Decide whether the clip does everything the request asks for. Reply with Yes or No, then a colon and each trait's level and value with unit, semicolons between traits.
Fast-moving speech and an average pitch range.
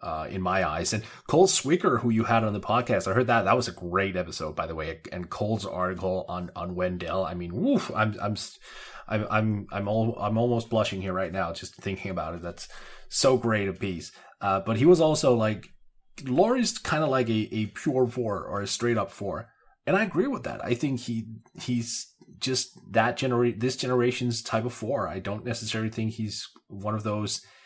Yes: fast, 215 wpm; average, 4.0 semitones